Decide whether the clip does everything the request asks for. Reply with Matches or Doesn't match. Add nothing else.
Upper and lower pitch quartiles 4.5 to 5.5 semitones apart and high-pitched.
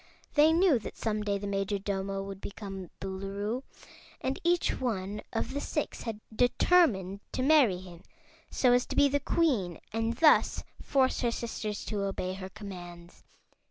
Matches